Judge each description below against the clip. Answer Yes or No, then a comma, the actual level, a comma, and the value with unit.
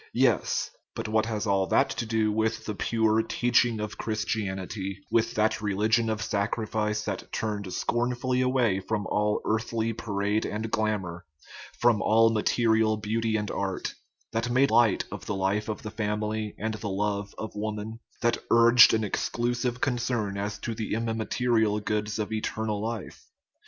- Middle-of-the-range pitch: No, low, 110 Hz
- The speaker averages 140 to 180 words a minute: Yes, average, 160 wpm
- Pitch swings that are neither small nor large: No, narrow, 1.6 semitones